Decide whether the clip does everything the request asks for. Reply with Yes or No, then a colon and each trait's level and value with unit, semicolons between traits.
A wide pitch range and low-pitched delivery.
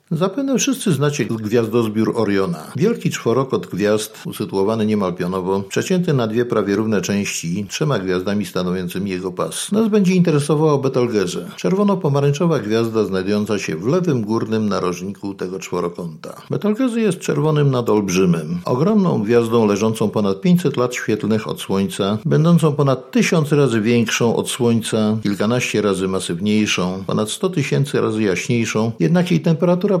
Yes: wide, 7.3 semitones; low, 120 Hz